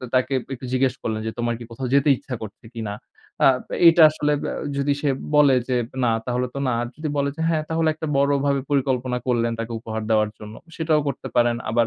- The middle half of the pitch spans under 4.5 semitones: Yes, average, 3.2 semitones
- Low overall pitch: Yes, low, 130 Hz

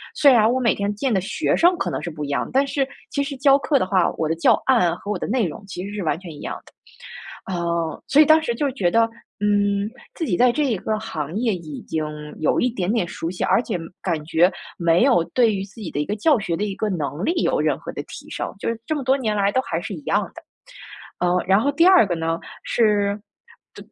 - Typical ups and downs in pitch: No, wide, 6.2 semitones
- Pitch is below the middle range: No, high, 205 Hz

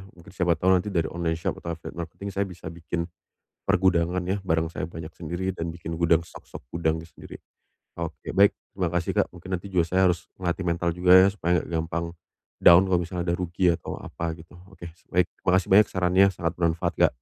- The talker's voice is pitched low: Yes, very low, 85 Hz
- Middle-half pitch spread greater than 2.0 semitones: No, narrow, 1.7 semitones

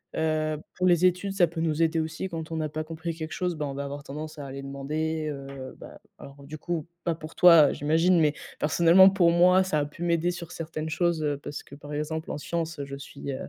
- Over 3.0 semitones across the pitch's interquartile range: No, narrow, 2.5 semitones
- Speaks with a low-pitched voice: No, medium, 160 Hz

